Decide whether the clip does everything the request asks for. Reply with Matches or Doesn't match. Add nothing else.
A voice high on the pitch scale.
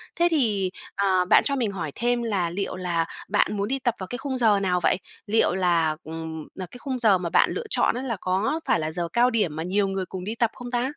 Matches